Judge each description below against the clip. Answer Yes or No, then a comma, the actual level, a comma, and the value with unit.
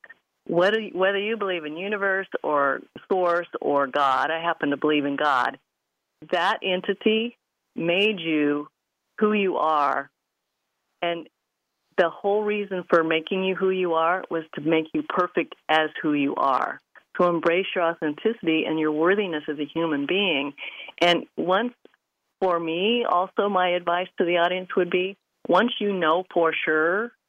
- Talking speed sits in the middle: Yes, average, 155 wpm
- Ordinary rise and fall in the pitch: Yes, average, 3.6 semitones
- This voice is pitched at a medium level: Yes, medium, 175 Hz